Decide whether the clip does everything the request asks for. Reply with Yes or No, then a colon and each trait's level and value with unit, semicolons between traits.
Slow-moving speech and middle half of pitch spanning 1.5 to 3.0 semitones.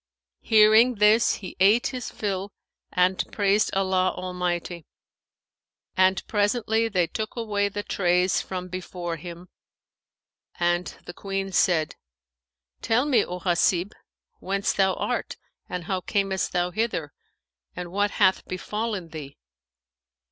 Yes: slow, 120 wpm; average, 2.7 semitones